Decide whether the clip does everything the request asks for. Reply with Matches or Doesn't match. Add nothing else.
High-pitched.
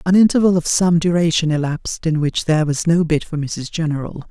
Doesn't match